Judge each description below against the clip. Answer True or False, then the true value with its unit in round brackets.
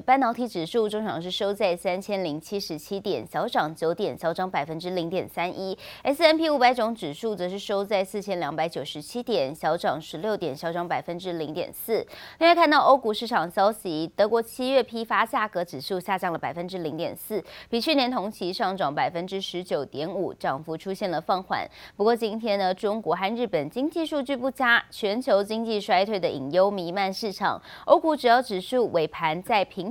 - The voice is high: True (200 Hz)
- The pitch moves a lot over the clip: False (4.8 semitones)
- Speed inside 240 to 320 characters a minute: True (305 characters per minute)